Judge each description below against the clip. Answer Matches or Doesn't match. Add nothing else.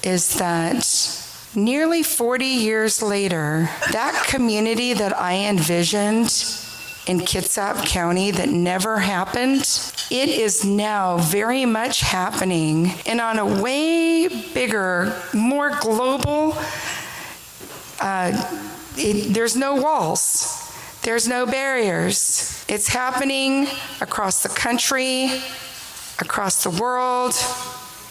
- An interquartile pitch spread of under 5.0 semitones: Doesn't match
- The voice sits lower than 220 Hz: Doesn't match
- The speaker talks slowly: Matches